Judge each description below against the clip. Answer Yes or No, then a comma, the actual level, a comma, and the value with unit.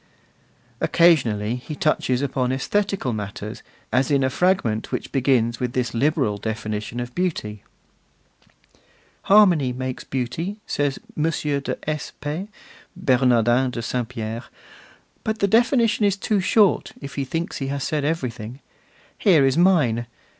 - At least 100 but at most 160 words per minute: Yes, slow, 135 wpm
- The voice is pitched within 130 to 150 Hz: Yes, low, 135 Hz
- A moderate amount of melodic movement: No, wide, 5.9 semitones